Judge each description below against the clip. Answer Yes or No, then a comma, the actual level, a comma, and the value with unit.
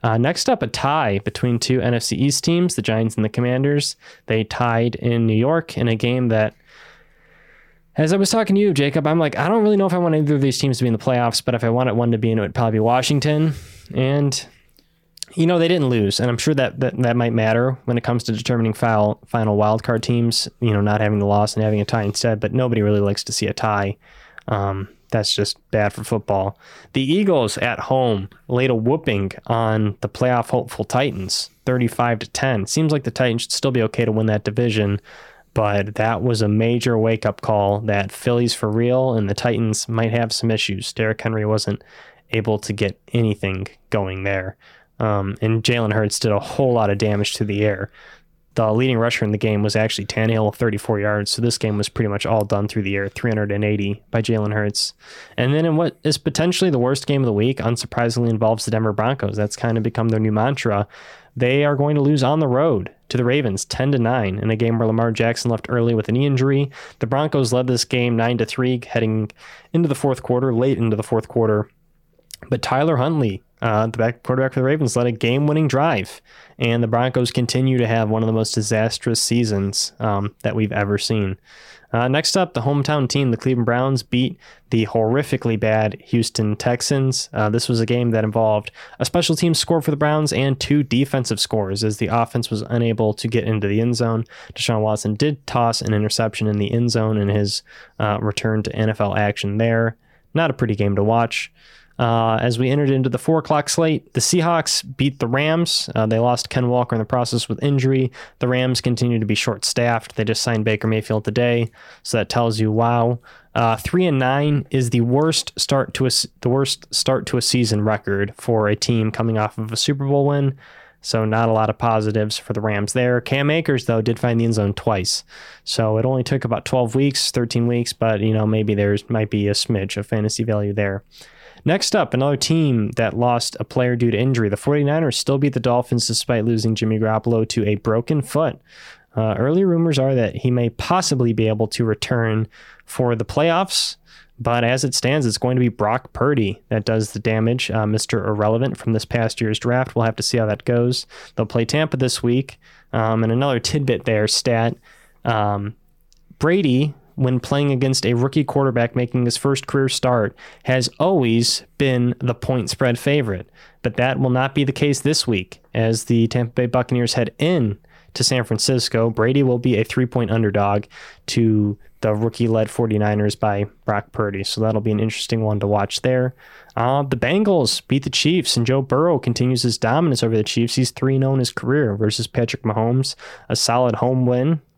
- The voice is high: No, low, 120 Hz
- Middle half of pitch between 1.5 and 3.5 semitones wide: Yes, average, 3.0 semitones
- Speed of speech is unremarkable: No, fast, 210 wpm